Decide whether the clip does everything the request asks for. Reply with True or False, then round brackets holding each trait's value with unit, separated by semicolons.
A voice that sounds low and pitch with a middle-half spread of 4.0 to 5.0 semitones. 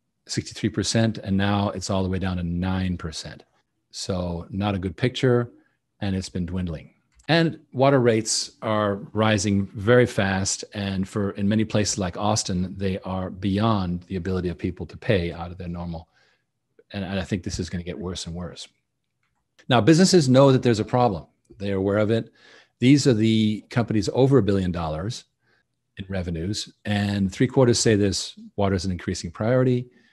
False (100 Hz; 3.6 semitones)